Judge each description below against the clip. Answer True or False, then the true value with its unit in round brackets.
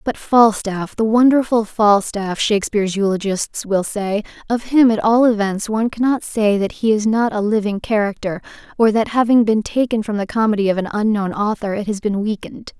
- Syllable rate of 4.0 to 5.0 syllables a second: False (5.3 syllables/s)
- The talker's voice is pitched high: True (215 Hz)